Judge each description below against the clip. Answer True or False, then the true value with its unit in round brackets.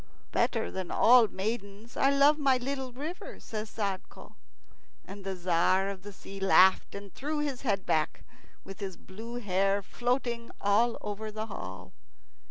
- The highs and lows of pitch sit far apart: False (4.1 semitones)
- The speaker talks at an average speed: True (155 wpm)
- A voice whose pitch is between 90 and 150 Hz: False (210 Hz)